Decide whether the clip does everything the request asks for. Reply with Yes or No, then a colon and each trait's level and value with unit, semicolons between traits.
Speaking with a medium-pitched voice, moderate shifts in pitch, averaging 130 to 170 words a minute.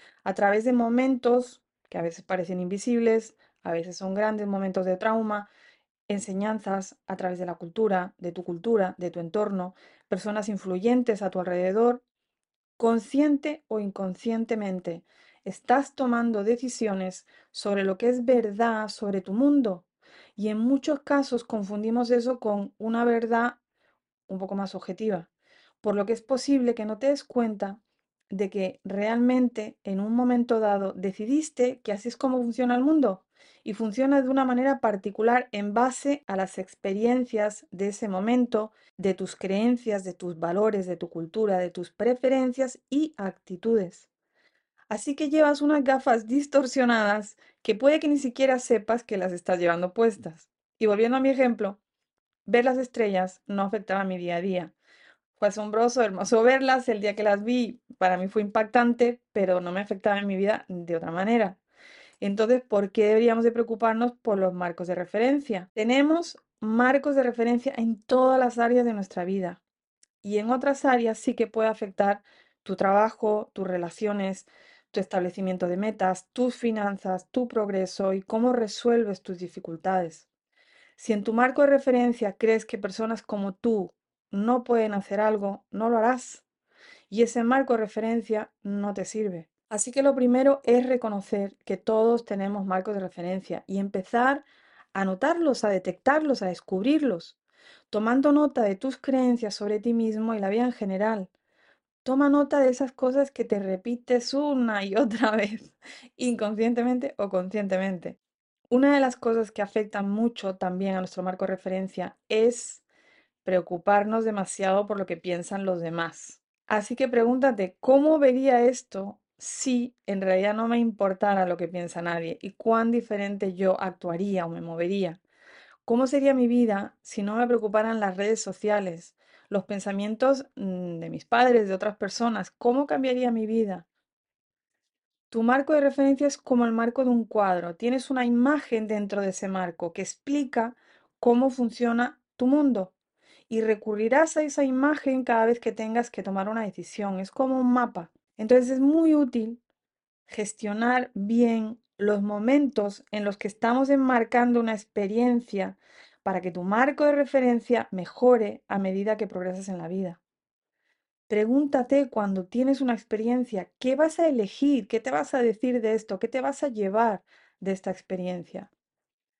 No: high, 220 Hz; average, 4.2 semitones; average, 160 wpm